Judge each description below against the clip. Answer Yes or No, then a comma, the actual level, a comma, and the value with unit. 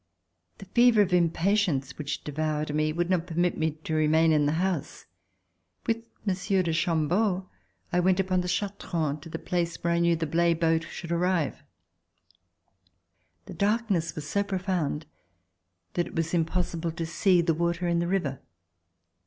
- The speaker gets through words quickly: No, average, 160 wpm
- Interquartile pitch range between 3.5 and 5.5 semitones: No, narrow, 2.5 semitones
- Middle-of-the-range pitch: Yes, medium, 170 Hz